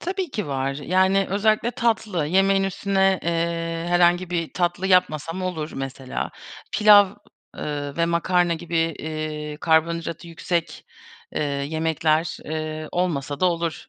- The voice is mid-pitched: Yes, medium, 170 Hz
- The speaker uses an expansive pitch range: No, average, 3.0 semitones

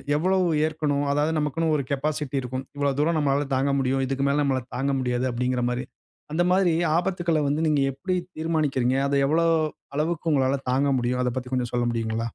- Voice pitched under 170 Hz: Yes, medium, 140 Hz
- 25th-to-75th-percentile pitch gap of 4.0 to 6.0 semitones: No, average, 3.3 semitones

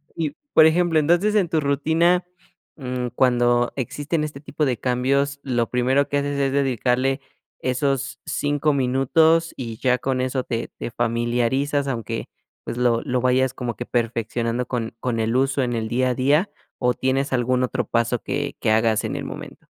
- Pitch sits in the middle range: No, low, 130 Hz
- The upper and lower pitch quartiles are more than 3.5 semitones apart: No, average, 2.7 semitones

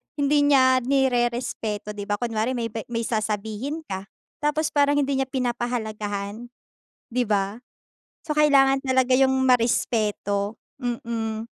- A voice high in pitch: Yes, high, 240 Hz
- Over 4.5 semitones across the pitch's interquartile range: No, average, 3.7 semitones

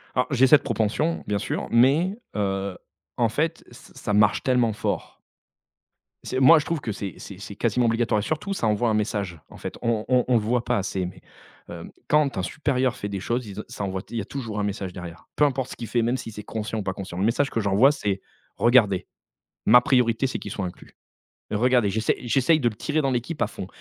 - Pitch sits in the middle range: No, low, 115 Hz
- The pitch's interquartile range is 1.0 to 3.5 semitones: No, average, 4.1 semitones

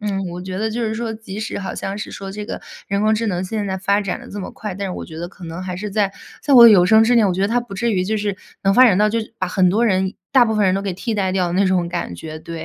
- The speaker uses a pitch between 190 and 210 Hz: Yes, high, 200 Hz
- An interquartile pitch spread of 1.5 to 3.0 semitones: Yes, average, 2.7 semitones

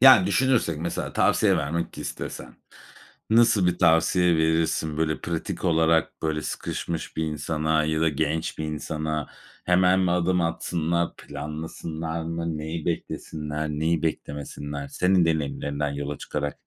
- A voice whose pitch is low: Yes, very low, 80 Hz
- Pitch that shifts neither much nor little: No, narrow, 1.9 semitones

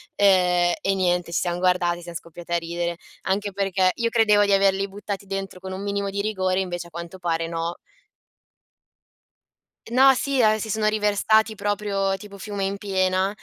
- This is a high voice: Yes, high, 195 Hz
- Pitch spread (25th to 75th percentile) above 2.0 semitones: Yes, narrow, 2.5 semitones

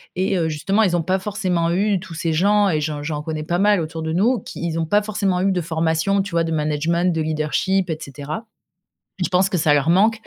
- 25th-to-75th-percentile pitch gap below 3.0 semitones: No, average, 3.4 semitones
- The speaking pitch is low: No, medium, 170 Hz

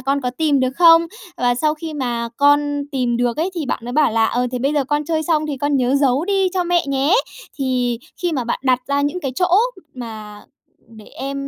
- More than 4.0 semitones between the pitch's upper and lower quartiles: No, average, 3.7 semitones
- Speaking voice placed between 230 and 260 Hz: No, very high, 275 Hz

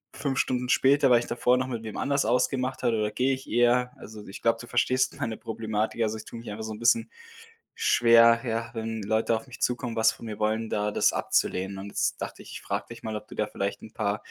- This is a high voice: No, low, 115 Hz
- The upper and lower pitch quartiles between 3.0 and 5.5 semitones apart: No, narrow, 2.5 semitones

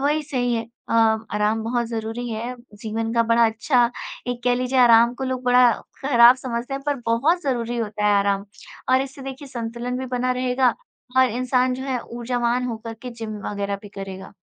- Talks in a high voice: Yes, high, 240 Hz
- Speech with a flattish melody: Yes, narrow, 2.0 semitones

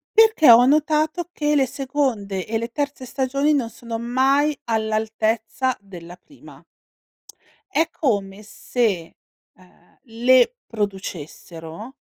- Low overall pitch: No, high, 235 Hz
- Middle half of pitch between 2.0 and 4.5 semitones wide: No, average, 5.0 semitones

